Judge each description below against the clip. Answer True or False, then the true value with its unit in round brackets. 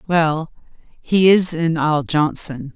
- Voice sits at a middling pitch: True (160 Hz)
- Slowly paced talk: True (130 wpm)